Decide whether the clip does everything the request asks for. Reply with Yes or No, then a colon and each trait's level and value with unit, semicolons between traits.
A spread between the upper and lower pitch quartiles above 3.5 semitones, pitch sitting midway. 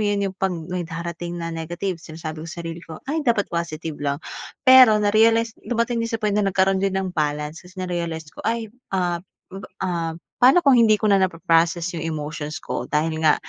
Yes: average, 4.3 semitones; medium, 180 Hz